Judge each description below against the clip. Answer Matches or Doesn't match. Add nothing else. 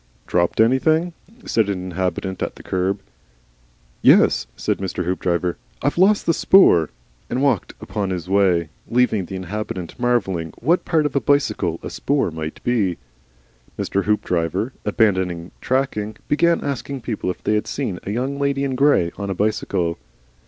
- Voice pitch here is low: Matches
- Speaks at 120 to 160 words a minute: Matches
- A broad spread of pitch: Matches